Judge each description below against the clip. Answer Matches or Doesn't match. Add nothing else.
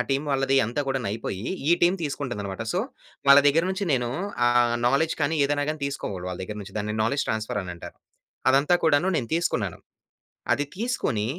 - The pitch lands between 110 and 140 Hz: Matches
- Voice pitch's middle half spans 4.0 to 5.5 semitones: Matches